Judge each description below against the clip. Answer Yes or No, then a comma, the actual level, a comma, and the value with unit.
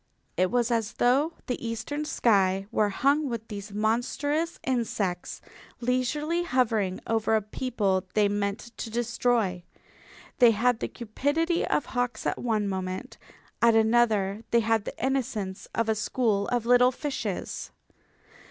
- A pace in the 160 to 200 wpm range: No, average, 140 wpm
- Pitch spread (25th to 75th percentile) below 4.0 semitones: Yes, average, 3.3 semitones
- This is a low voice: No, high, 230 Hz